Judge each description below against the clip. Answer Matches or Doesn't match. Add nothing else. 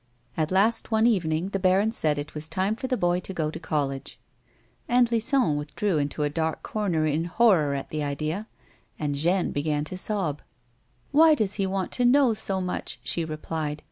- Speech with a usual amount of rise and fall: Doesn't match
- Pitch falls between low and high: Matches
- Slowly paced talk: Doesn't match